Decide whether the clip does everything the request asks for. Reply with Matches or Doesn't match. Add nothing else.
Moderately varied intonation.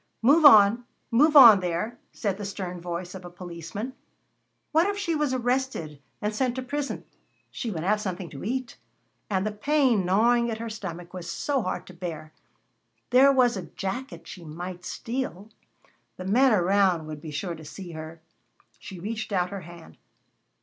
Doesn't match